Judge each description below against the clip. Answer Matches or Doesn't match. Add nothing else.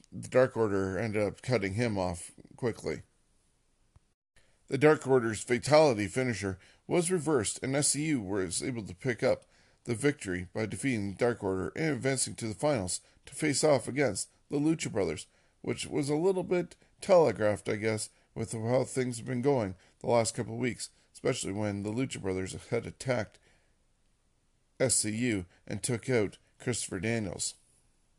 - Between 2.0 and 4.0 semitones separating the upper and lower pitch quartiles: Doesn't match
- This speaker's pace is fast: Doesn't match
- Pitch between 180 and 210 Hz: Doesn't match